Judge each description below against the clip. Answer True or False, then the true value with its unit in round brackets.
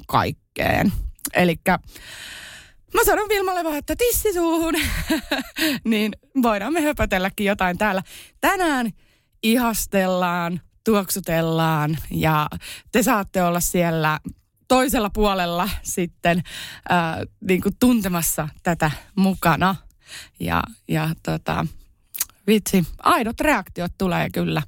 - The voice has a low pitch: False (195 Hz)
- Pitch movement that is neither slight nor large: False (6.9 semitones)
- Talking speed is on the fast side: False (95 wpm)